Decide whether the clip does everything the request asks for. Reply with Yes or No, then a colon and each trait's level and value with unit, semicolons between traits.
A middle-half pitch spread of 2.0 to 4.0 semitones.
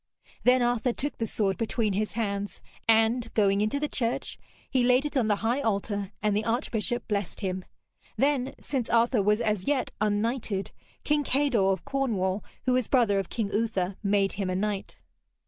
Yes: average, 3.6 semitones